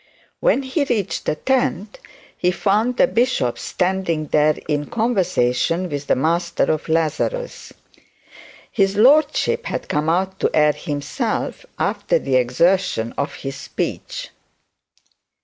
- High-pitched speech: No, medium, 180 Hz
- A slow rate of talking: Yes, slow, 125 wpm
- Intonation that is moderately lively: No, wide, 6.8 semitones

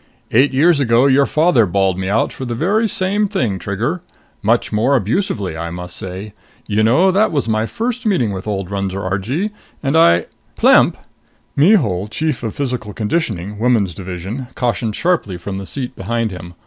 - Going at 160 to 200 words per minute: Yes, average, 175 wpm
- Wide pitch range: Yes, wide, 6.9 semitones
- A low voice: Yes, low, 115 Hz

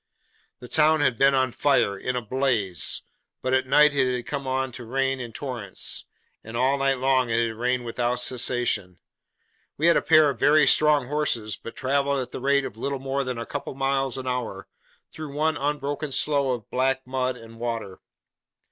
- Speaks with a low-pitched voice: Yes, low, 130 Hz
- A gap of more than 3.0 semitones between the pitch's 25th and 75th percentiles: No, narrow, 2.5 semitones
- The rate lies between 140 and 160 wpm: No, average, 195 wpm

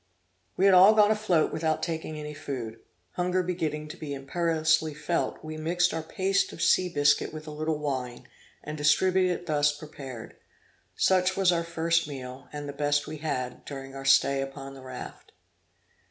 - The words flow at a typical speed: Yes, average, 175 wpm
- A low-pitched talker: No, medium, 155 Hz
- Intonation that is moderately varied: Yes, average, 3.5 semitones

